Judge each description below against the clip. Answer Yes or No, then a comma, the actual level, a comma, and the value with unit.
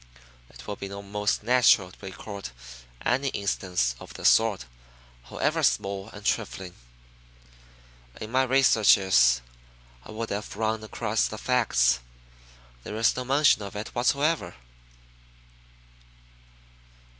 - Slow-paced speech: Yes, slow, 115 wpm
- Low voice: Yes, low, 105 Hz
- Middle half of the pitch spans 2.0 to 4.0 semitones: Yes, average, 3.4 semitones